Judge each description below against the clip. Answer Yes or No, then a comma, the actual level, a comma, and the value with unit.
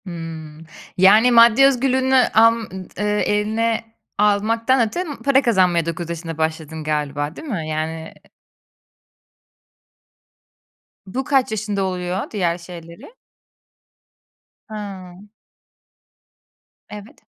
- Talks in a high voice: Yes, high, 200 Hz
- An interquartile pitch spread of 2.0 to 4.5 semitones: No, average, 5.3 semitones